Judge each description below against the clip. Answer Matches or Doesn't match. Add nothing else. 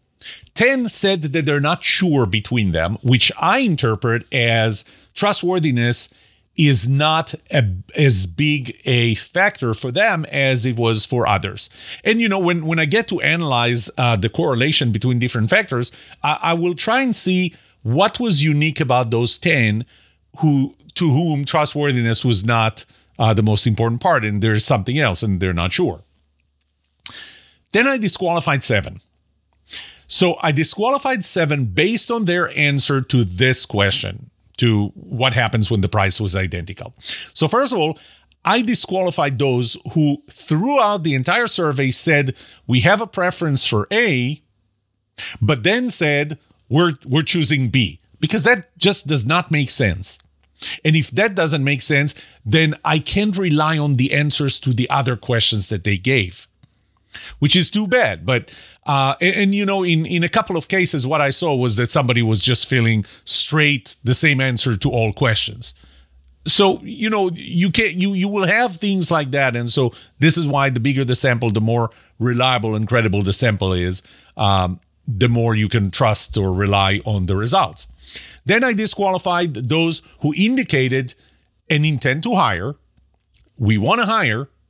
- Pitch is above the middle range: Doesn't match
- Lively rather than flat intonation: Matches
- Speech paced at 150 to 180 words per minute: Matches